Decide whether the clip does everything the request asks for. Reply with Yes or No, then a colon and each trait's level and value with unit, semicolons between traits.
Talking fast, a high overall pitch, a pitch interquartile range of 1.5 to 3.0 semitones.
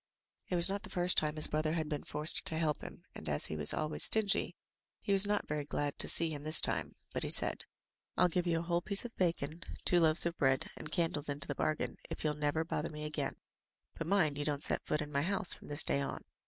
No: fast, 255 wpm; medium, 155 Hz; average, 2.7 semitones